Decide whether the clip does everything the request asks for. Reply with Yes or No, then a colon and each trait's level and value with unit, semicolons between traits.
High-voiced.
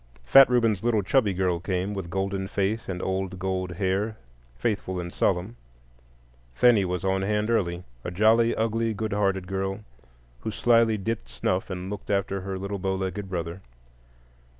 No: very low, 95 Hz